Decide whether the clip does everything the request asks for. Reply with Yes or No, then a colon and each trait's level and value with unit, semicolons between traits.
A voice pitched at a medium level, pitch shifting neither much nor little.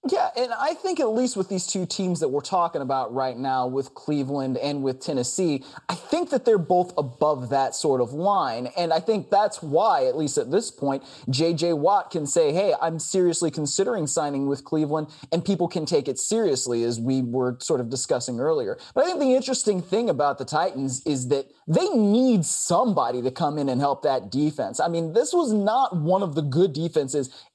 No: medium, 165 Hz; wide, 6.9 semitones